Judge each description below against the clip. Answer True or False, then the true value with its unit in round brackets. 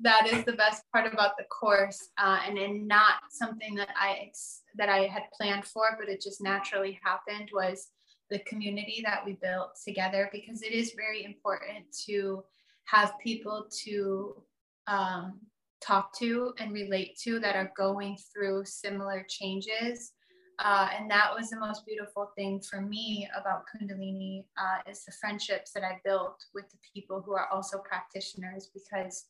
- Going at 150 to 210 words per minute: True (165 wpm)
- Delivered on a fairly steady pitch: True (1.5 semitones)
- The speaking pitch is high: True (200 Hz)